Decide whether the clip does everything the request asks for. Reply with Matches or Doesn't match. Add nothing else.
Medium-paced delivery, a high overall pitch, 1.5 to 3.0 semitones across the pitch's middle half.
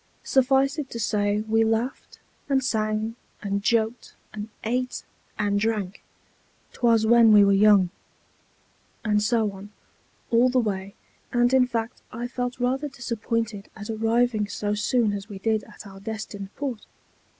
Matches